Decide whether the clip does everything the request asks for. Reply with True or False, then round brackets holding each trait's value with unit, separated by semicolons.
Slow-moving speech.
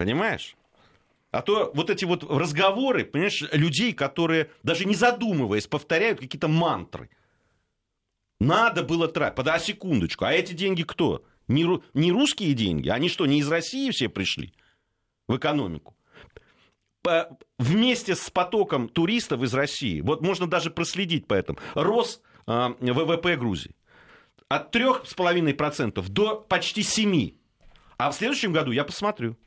False (135 wpm)